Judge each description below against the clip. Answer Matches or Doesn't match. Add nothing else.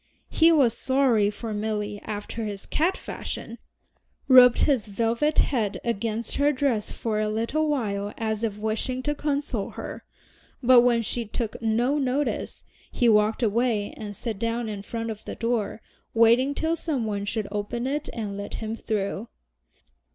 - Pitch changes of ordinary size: Matches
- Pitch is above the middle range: Matches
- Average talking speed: Matches